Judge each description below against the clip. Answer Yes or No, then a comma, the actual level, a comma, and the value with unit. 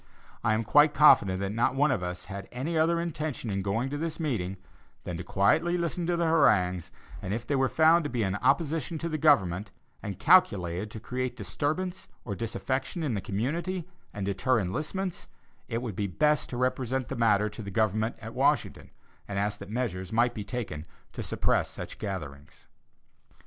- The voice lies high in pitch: No, low, 120 Hz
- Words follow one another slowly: No, average, 190 wpm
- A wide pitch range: Yes, wide, 7.2 semitones